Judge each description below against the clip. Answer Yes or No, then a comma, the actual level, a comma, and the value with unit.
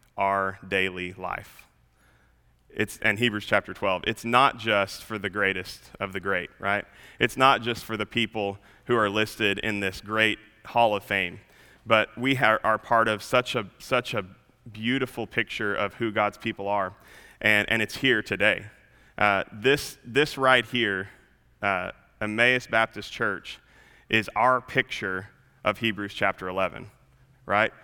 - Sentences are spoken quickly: No, average, 155 wpm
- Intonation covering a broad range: No, average, 3.3 semitones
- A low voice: Yes, low, 110 Hz